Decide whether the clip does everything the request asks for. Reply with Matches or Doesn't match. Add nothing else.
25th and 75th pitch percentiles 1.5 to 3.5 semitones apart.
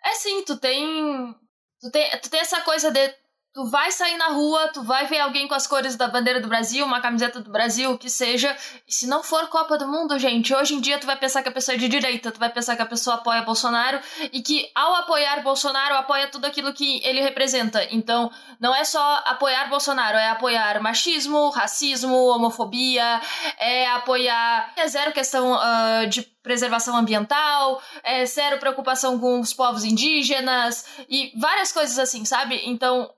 Matches